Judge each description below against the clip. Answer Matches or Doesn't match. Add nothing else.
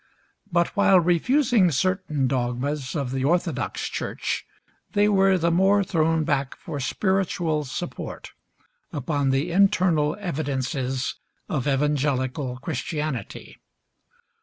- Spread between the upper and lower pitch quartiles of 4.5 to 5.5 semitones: Matches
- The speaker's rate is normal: Doesn't match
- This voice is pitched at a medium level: Matches